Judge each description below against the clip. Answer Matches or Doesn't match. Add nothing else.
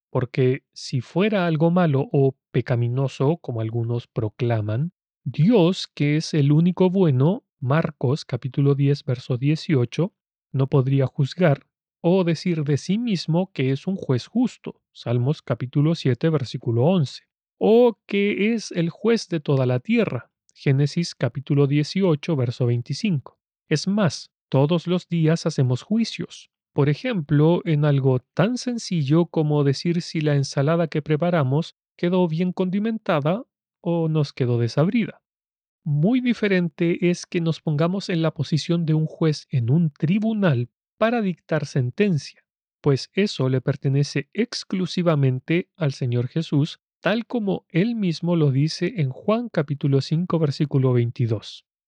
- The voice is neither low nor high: Matches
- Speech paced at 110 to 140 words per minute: Matches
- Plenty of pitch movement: Doesn't match